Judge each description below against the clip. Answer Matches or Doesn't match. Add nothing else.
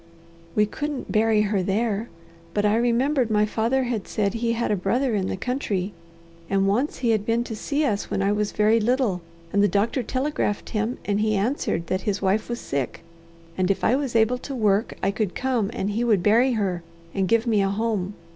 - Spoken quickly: Matches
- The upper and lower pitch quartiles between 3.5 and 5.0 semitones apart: Doesn't match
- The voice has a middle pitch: Doesn't match